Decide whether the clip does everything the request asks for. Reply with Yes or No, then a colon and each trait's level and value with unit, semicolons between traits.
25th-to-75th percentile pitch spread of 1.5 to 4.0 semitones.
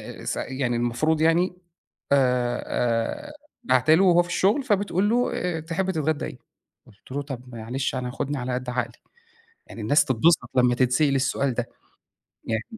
No: average, 5.2 semitones